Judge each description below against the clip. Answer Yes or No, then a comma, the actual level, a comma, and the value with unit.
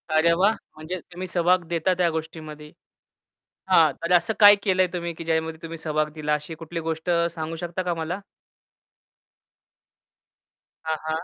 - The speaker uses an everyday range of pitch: No, narrow, 2.0 semitones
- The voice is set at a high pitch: No, medium, 165 Hz